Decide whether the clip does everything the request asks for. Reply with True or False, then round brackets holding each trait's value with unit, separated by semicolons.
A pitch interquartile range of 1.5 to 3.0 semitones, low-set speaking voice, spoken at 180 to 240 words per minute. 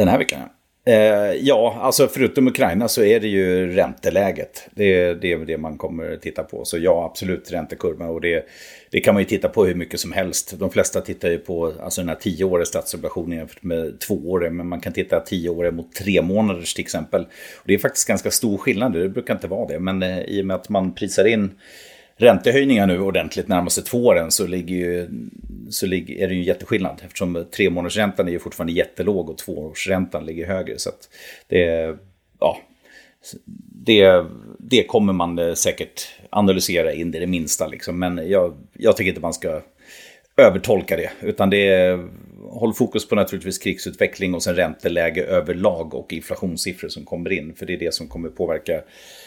True (2.6 semitones; 90 Hz; 190 wpm)